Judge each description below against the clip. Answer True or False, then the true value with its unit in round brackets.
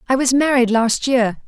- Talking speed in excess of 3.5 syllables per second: True (4.6 syllables/s)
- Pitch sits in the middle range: False (250 Hz)